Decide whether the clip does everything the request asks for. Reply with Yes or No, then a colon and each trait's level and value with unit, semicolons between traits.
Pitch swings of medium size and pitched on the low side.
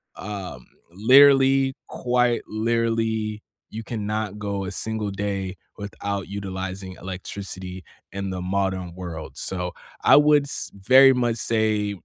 Yes: average, 3.4 semitones; low, 105 Hz